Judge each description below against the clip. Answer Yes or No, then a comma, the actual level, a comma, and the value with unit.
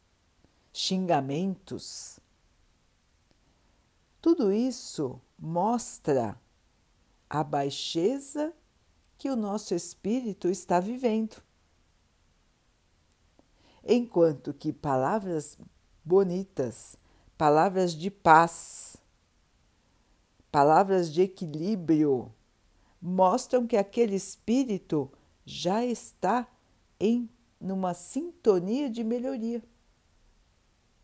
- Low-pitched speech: No, medium, 180 Hz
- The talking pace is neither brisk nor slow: No, slow, 65 wpm